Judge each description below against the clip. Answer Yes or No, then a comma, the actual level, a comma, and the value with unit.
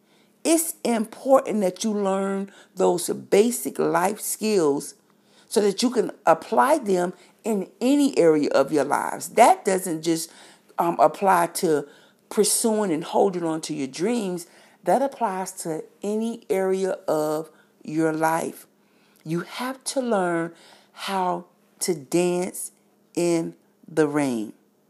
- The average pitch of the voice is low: No, high, 190 Hz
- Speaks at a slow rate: Yes, slow, 125 wpm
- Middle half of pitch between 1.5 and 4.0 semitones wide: No, average, 4.6 semitones